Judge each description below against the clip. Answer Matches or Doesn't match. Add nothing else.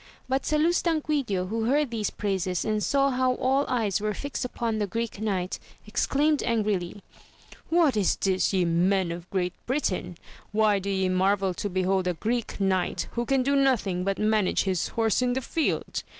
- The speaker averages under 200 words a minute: Matches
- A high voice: Matches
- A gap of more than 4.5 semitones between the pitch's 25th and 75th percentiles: Matches